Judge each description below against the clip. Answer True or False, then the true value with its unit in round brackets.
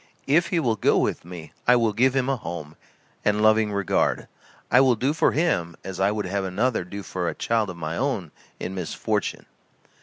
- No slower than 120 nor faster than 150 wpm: False (205 wpm)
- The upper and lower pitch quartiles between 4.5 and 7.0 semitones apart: True (5.6 semitones)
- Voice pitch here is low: True (105 Hz)